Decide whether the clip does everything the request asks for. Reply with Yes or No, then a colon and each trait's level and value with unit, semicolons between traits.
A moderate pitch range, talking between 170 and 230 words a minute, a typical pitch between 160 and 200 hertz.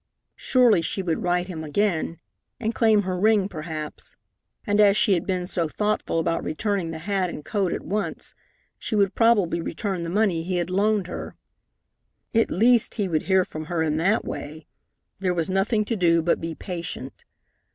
Yes: average, 3.9 semitones; average, 185 wpm; medium, 185 Hz